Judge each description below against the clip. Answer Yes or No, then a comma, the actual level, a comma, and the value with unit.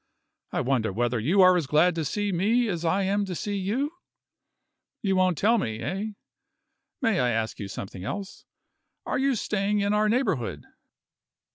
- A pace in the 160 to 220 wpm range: Yes, average, 170 wpm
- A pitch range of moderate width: No, wide, 7.4 semitones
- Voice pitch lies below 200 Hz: Yes, high, 190 Hz